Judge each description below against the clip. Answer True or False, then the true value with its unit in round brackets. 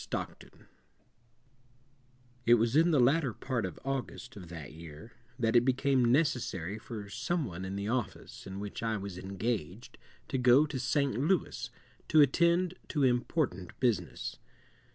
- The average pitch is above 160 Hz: False (120 Hz)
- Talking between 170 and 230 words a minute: False (155 wpm)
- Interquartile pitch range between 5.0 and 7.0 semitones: True (5.6 semitones)